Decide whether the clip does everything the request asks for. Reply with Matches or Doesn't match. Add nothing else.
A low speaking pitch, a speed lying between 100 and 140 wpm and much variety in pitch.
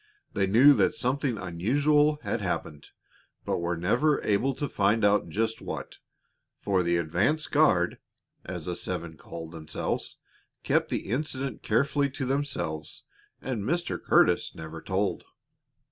Matches